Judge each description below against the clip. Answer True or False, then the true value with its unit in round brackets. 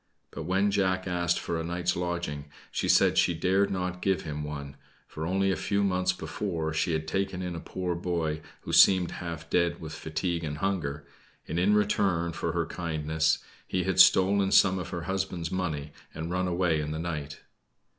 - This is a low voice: True (85 Hz)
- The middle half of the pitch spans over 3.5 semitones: False (2.8 semitones)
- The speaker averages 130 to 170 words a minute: False (190 wpm)